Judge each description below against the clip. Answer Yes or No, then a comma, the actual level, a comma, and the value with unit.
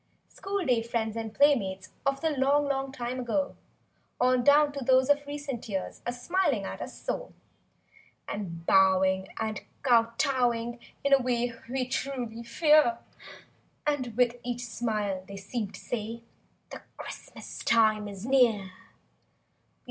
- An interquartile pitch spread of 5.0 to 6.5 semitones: No, average, 3.8 semitones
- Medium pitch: No, high, 240 Hz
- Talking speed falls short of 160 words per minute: Yes, average, 140 wpm